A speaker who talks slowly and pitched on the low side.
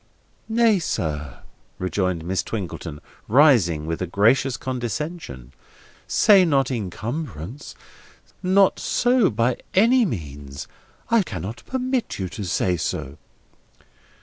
Yes: slow, 105 wpm; low, 115 Hz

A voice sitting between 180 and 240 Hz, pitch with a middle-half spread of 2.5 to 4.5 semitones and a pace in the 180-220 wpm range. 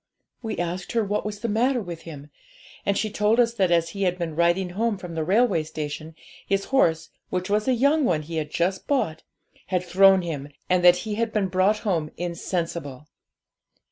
Yes: medium, 185 Hz; average, 4.1 semitones; average, 200 wpm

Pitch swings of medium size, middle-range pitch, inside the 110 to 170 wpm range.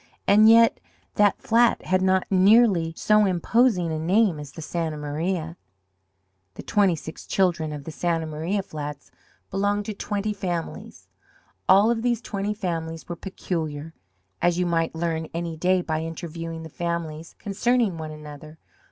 Yes: average, 3.8 semitones; medium, 175 Hz; average, 150 wpm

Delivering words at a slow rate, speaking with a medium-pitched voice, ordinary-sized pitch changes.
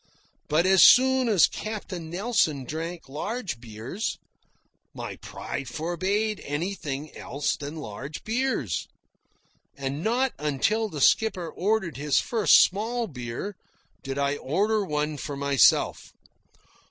No: slow, 115 wpm; medium, 165 Hz; wide, 7.1 semitones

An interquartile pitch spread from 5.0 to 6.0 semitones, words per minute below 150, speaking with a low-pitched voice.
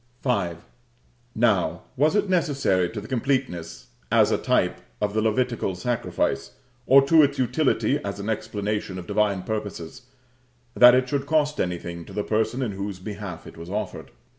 No: wide, 5.5 semitones; average, 165 wpm; low, 110 Hz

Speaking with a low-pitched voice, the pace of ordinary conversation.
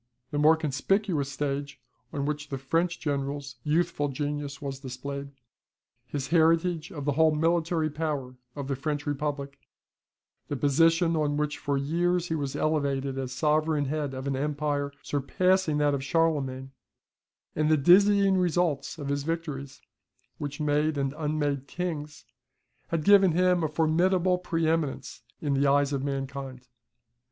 No: medium, 150 Hz; average, 145 wpm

